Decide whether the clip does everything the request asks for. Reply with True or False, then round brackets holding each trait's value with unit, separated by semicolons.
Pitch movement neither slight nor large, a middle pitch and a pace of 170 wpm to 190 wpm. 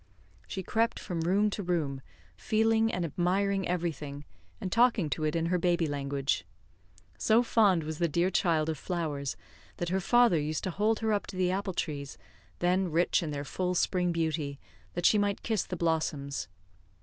True (4.1 semitones; 175 Hz; 180 wpm)